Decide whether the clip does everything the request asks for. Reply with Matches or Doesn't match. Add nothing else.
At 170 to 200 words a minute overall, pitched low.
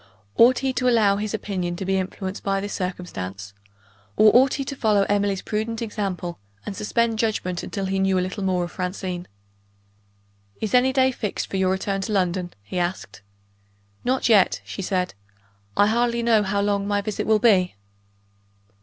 Doesn't match